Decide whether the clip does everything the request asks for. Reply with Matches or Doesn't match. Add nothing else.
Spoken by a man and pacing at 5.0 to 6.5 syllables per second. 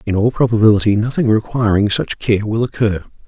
Matches